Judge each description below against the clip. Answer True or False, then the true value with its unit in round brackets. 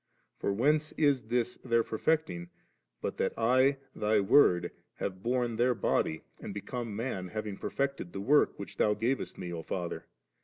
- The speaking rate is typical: True (160 wpm)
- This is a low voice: True (115 Hz)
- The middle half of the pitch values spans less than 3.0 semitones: False (4.8 semitones)